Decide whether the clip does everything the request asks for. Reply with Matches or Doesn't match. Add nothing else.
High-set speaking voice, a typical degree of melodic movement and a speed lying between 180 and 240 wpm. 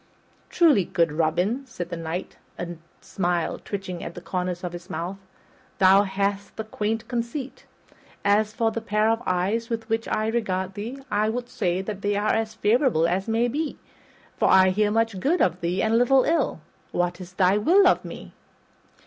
Matches